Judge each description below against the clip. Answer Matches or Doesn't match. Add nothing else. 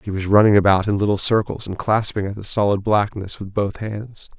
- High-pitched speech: Doesn't match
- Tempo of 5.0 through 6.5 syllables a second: Matches